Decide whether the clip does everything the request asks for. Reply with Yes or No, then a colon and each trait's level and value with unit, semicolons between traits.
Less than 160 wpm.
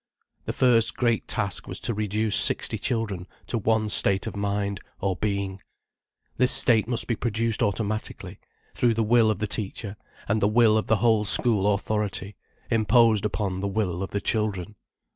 No: average, 170 wpm